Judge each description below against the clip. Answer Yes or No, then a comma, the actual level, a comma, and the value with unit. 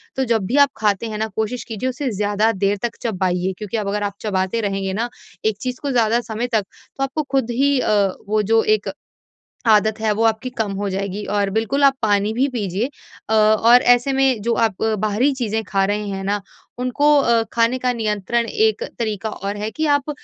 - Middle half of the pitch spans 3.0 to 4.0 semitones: Yes, average, 3.4 semitones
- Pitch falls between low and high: No, high, 220 Hz